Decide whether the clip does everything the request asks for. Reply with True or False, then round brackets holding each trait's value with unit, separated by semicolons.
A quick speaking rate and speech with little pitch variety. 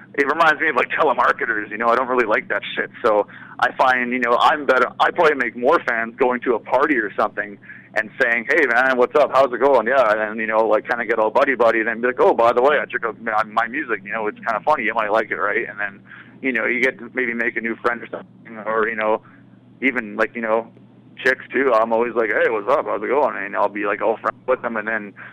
True (280 wpm; 2.3 semitones)